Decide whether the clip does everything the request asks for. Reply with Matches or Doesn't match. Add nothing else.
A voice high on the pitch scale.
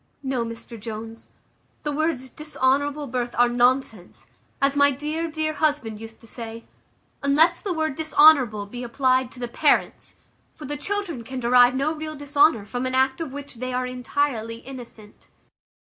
Matches